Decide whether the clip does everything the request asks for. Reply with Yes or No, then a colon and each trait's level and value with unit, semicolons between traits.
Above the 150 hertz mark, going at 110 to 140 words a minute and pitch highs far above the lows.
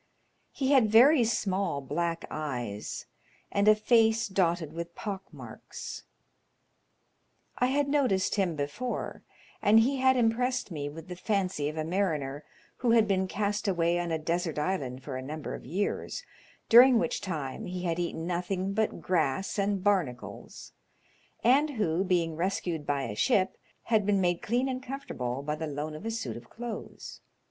No: medium, 185 Hz; average, 165 wpm; wide, 6.0 semitones